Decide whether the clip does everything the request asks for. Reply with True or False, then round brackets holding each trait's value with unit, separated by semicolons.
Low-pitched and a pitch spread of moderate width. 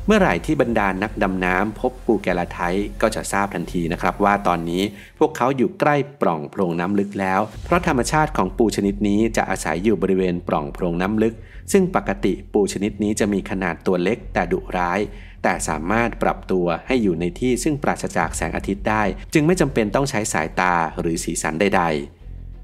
True (100 Hz; 4.2 semitones)